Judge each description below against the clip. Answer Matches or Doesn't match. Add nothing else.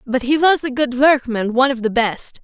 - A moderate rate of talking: Doesn't match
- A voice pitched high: Matches